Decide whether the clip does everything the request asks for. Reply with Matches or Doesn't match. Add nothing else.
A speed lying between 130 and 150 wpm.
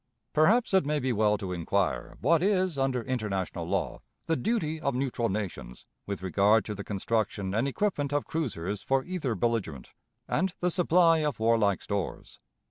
Doesn't match